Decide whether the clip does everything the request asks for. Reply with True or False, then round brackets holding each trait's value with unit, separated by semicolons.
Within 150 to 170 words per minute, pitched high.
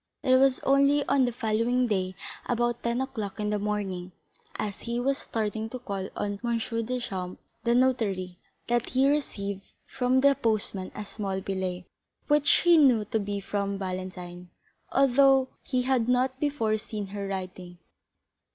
True (160 wpm; 225 Hz)